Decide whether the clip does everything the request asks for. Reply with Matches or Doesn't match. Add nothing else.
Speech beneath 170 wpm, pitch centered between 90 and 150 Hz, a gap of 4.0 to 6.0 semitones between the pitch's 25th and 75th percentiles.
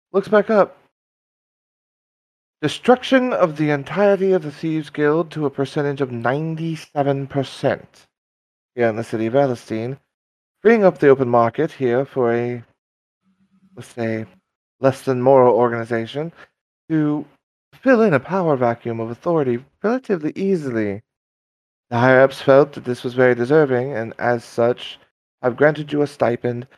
Matches